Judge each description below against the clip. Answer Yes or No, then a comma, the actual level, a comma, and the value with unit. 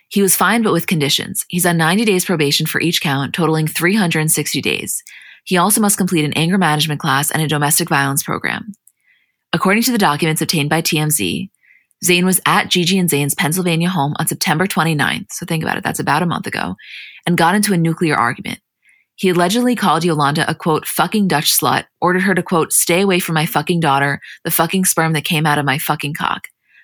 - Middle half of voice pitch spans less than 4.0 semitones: Yes, average, 3.4 semitones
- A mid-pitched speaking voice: Yes, medium, 165 Hz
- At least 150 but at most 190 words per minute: No, fast, 205 wpm